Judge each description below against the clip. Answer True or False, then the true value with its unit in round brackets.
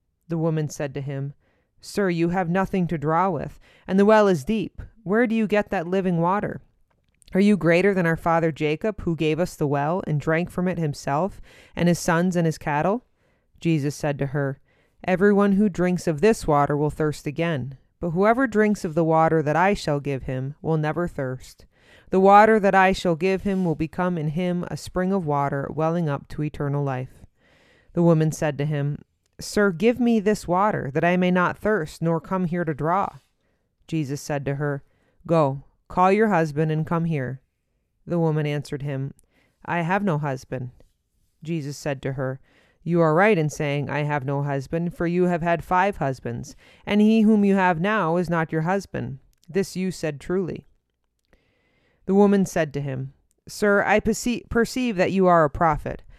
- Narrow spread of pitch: False (4.3 semitones)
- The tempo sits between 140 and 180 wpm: False (190 wpm)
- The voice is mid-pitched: True (165 Hz)